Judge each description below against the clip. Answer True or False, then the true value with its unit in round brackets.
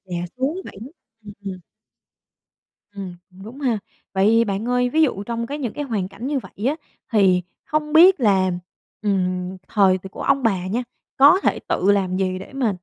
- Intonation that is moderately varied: False (5.8 semitones)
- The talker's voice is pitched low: False (210 Hz)